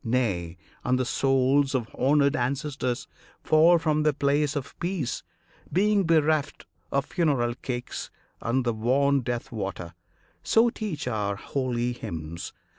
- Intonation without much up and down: No, average, 4.0 semitones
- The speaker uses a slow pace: Yes, slow, 130 wpm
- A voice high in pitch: No, low, 135 Hz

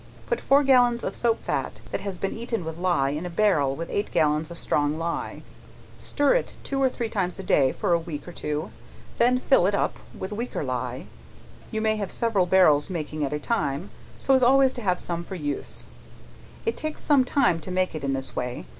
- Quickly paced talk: Yes, fast, 215 wpm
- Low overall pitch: No, medium, 185 Hz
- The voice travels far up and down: Yes, wide, 7.6 semitones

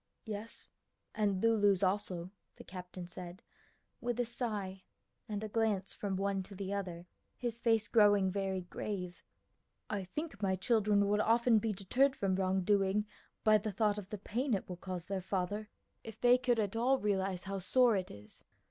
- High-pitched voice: Yes, high, 200 Hz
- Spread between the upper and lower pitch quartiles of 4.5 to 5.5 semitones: No, average, 2.7 semitones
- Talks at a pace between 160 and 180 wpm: Yes, average, 175 wpm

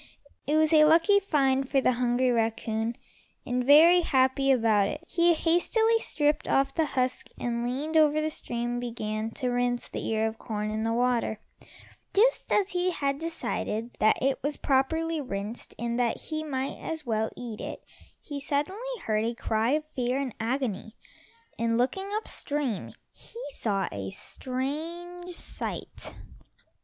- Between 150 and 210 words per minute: Yes, average, 160 wpm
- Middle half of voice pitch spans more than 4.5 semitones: Yes, average, 5.1 semitones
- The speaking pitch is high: Yes, very high, 260 Hz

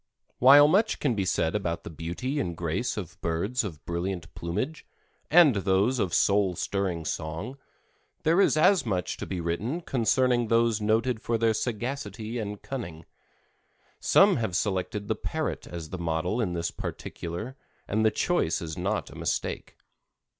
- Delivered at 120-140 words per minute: No, average, 160 wpm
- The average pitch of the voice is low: Yes, low, 105 Hz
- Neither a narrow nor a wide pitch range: No, wide, 6.3 semitones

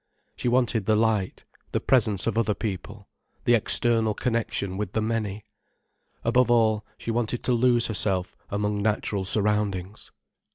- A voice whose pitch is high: No, low, 110 Hz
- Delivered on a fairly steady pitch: Yes, narrow, 2.2 semitones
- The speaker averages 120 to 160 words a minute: Yes, average, 140 wpm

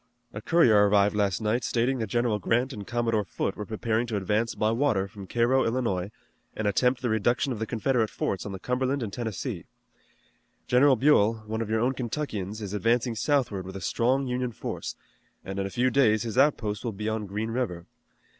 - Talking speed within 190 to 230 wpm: Yes, average, 200 wpm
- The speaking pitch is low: Yes, low, 110 Hz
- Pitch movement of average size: Yes, average, 3.2 semitones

